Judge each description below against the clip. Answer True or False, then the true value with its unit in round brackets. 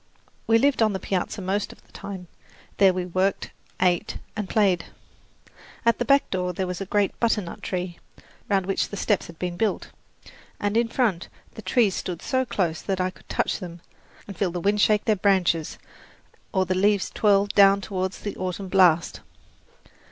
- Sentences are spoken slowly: False (180 wpm)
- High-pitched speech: True (195 Hz)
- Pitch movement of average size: False (2.3 semitones)